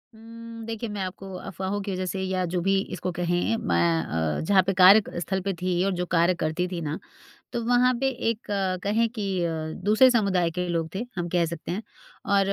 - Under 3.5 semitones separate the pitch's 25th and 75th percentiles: No, average, 3.8 semitones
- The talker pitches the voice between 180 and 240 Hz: Yes, high, 190 Hz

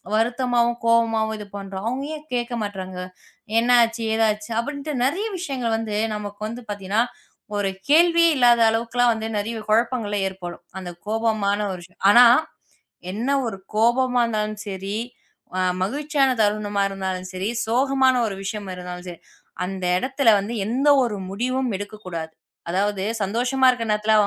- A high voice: Yes, high, 220 Hz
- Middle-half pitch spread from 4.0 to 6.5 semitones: No, average, 3.6 semitones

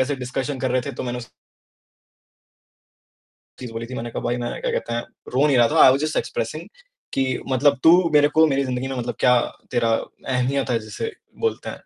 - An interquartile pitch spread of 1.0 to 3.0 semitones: Yes, narrow, 2.4 semitones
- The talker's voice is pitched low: Yes, low, 130 Hz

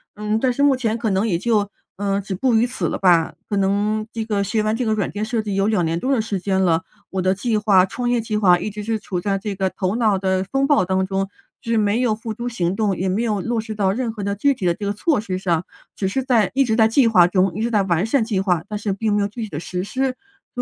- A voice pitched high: Yes, high, 210 Hz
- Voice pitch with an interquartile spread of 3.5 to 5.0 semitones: No, average, 2.9 semitones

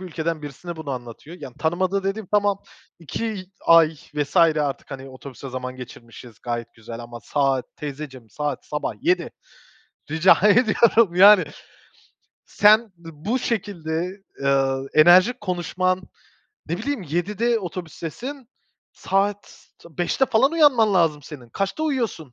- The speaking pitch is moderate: Yes, medium, 170 Hz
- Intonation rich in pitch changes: Yes, wide, 6.6 semitones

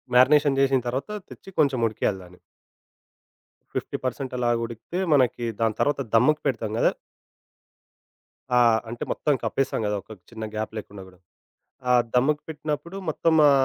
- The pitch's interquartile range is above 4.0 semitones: Yes, average, 4.4 semitones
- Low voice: Yes, low, 125 Hz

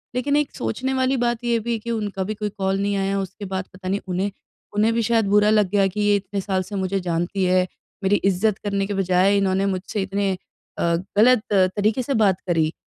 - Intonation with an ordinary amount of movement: No, narrow, 2.2 semitones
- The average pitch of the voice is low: No, high, 200 Hz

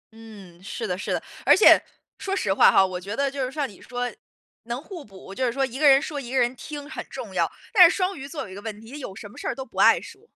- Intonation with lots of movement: Yes, wide, 5.9 semitones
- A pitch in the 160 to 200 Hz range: No, very high, 255 Hz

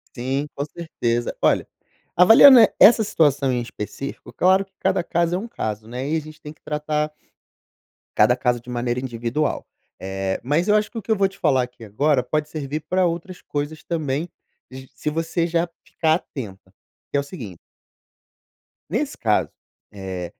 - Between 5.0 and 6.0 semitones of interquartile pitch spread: Yes, wide, 5.6 semitones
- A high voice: No, medium, 150 Hz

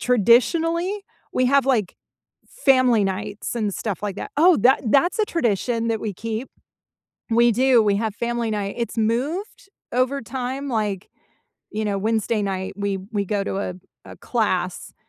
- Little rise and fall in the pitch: No, average, 4.1 semitones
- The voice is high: Yes, high, 230 Hz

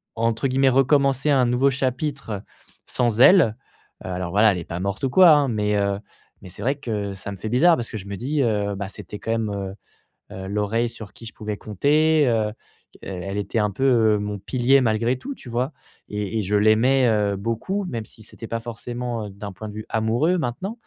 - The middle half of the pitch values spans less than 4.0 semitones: No, average, 4.3 semitones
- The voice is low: Yes, low, 115 Hz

